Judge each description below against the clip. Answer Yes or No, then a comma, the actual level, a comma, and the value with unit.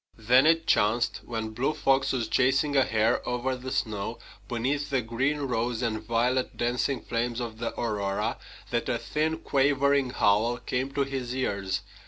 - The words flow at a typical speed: Yes, average, 165 wpm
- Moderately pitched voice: No, low, 125 Hz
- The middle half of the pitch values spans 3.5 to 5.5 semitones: No, average, 3.0 semitones